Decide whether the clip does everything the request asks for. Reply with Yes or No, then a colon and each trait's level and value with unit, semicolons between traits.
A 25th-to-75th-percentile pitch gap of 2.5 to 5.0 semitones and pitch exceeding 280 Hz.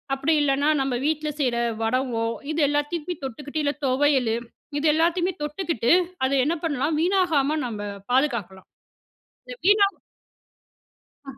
Yes: average, 3.9 semitones; very high, 290 Hz